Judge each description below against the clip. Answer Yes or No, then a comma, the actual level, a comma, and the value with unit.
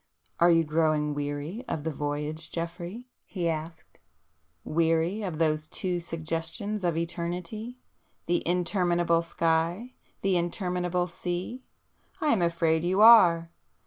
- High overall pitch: No, medium, 170 Hz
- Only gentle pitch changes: Yes, narrow, 2.0 semitones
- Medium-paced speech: No, slow, 115 wpm